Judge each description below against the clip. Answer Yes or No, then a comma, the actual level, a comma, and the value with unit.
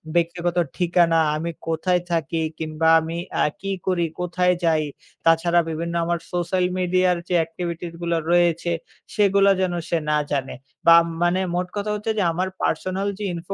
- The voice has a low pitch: No, medium, 175 Hz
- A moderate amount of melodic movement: No, narrow, 1.7 semitones